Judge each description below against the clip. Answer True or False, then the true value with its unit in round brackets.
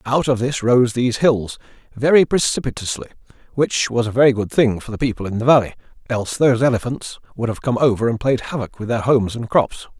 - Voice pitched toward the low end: True (120 Hz)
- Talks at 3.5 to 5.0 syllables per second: False (6.1 syllables/s)